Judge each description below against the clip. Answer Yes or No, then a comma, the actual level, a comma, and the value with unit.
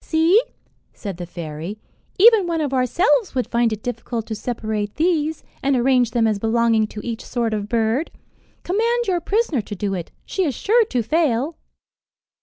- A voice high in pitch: Yes, high, 245 Hz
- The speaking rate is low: No, average, 175 wpm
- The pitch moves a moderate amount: No, wide, 7.2 semitones